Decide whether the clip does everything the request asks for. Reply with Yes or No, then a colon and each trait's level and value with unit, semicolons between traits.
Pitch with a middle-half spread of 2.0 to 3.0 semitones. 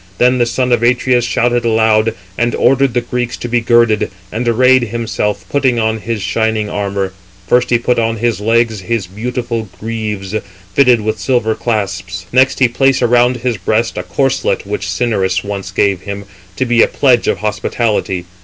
Yes: narrow, 2.5 semitones